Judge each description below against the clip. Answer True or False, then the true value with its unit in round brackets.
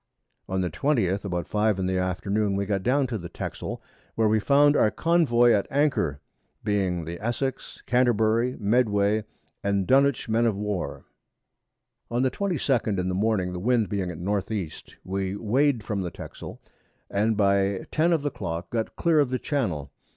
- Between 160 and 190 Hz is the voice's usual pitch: False (105 Hz)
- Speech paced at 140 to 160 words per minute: False (175 wpm)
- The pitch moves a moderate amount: True (4.7 semitones)